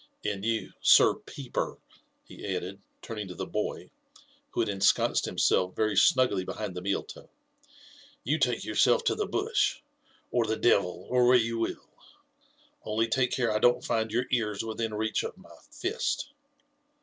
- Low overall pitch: Yes, low, 110 Hz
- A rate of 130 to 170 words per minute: Yes, average, 160 wpm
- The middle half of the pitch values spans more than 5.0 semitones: No, average, 3.2 semitones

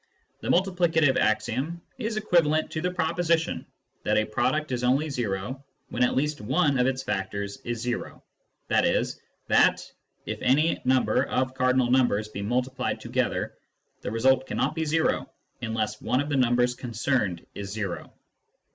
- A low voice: Yes, low, 130 Hz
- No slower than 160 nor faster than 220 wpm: No, average, 150 wpm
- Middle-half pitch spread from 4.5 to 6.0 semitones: Yes, average, 5.0 semitones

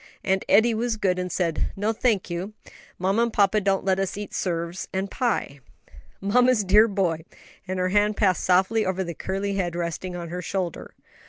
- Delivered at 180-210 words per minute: Yes, average, 185 wpm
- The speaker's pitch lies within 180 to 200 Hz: Yes, high, 190 Hz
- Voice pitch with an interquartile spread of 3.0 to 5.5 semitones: No, narrow, 2.5 semitones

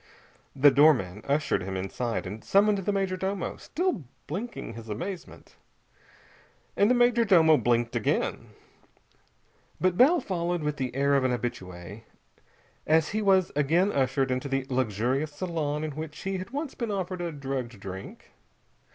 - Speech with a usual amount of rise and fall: No, wide, 7.4 semitones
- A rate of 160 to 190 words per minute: No, average, 150 wpm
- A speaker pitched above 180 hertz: No, medium, 150 Hz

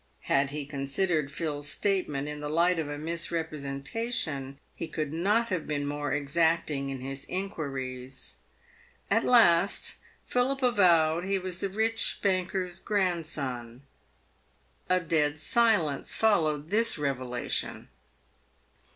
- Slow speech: Yes, slow, 115 wpm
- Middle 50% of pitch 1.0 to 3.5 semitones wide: No, average, 4.9 semitones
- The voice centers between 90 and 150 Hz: No, medium, 160 Hz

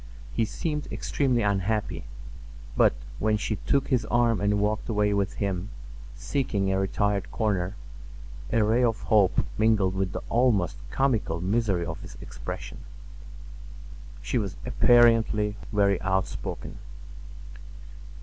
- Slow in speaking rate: Yes, slow, 120 wpm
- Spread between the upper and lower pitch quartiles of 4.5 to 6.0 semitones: No, average, 2.9 semitones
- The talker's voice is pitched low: Yes, low, 105 Hz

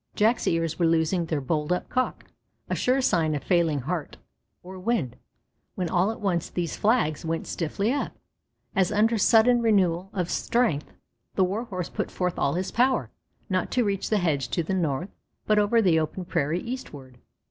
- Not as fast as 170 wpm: No, average, 180 wpm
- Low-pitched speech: No, medium, 180 Hz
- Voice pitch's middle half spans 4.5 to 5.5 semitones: Yes, average, 4.8 semitones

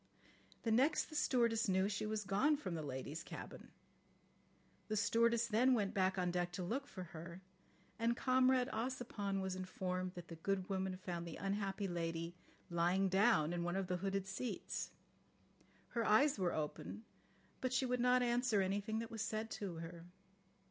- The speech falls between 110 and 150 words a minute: No, average, 170 wpm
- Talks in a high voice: Yes, high, 195 Hz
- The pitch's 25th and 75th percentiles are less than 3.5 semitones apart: No, average, 4.4 semitones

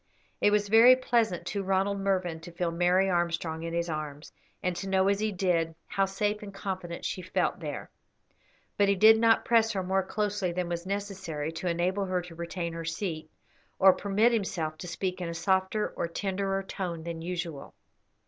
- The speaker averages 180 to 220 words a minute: Yes, average, 190 wpm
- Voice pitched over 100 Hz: Yes, medium, 185 Hz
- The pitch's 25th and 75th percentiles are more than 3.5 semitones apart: No, average, 2.8 semitones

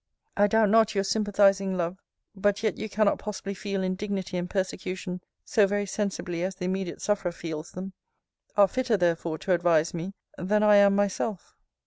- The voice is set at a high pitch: Yes, high, 195 Hz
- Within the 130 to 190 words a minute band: Yes, average, 170 wpm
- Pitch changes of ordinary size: No, narrow, 2.2 semitones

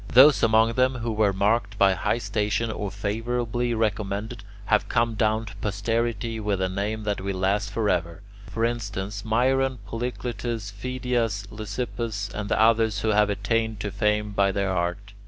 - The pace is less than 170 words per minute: Yes, average, 160 wpm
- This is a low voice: Yes, low, 105 Hz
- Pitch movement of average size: No, narrow, 2.3 semitones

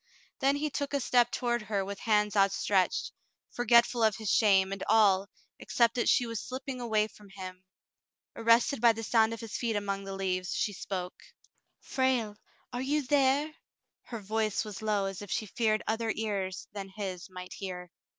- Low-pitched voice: No, high, 215 Hz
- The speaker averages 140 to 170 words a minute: No, average, 180 wpm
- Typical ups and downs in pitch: Yes, average, 3.4 semitones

